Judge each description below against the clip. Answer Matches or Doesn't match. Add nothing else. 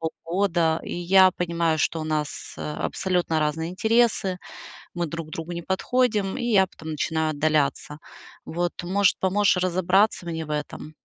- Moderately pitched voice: Matches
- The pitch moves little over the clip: Doesn't match